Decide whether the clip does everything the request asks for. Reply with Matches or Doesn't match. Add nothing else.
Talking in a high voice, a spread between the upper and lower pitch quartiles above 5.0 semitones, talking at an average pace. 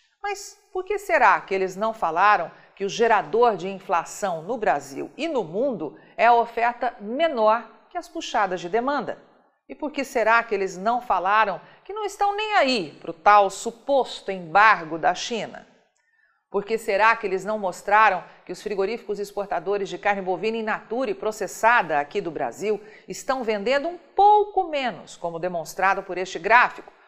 Matches